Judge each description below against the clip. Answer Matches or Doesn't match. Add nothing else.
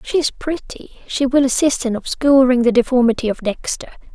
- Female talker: Matches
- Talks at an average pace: Matches